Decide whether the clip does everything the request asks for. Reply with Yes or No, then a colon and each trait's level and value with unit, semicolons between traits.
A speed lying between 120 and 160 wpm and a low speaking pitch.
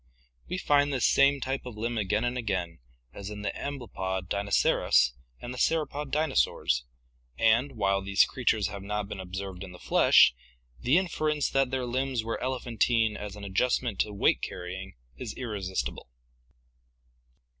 Yes: average, 155 wpm; low, 110 Hz